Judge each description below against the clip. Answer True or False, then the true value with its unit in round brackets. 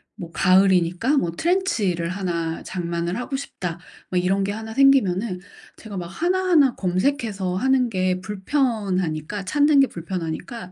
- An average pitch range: False (6.2 semitones)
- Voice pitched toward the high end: True (195 Hz)